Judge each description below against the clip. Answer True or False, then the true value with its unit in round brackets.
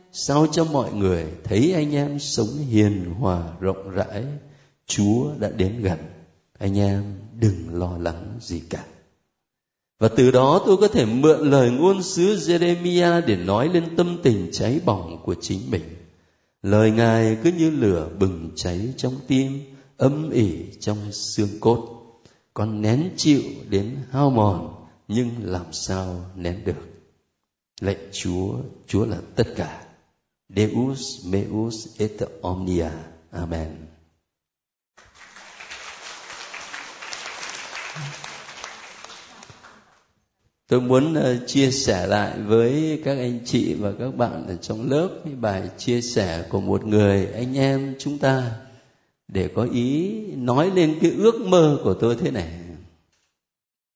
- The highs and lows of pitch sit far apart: True (6.5 semitones)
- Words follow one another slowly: True (130 wpm)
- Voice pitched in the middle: False (110 Hz)